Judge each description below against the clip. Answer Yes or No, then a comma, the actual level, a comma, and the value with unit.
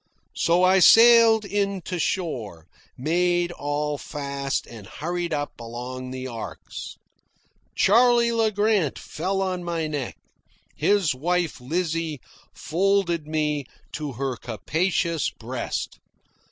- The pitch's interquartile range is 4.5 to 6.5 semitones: Yes, wide, 5.5 semitones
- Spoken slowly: Yes, slow, 115 wpm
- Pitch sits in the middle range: Yes, medium, 165 Hz